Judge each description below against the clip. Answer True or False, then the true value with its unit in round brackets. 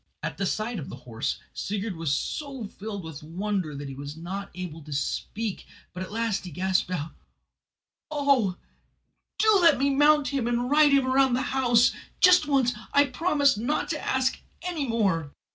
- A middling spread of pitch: False (7.4 semitones)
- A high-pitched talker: True (225 Hz)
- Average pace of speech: True (180 wpm)